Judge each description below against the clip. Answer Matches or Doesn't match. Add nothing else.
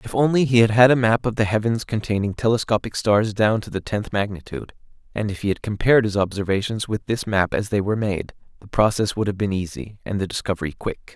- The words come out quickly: Matches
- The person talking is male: Matches